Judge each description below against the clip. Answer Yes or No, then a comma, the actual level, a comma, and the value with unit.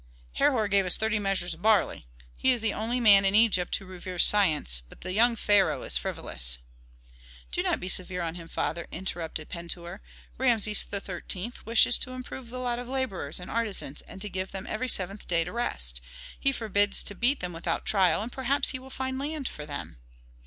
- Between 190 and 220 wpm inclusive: Yes, average, 195 wpm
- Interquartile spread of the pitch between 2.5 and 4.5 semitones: No, average, 5.0 semitones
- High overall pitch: Yes, high, 200 Hz